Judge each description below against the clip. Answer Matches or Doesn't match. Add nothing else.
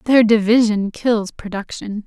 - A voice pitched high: Matches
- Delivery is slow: Matches